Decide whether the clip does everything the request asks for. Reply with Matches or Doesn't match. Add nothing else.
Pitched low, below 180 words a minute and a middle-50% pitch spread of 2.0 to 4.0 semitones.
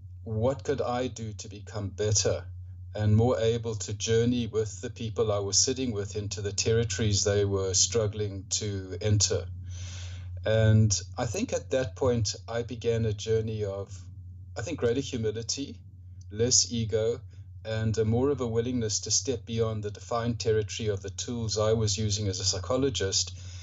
Matches